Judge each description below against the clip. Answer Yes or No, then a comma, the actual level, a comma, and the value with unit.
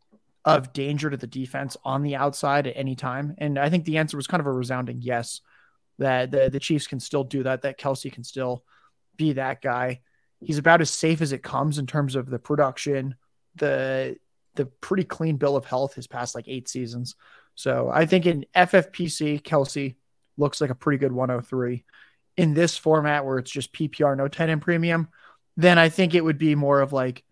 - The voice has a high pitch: No, medium, 140 Hz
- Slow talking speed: No, fast, 205 wpm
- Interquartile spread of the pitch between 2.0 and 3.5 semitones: Yes, average, 3.0 semitones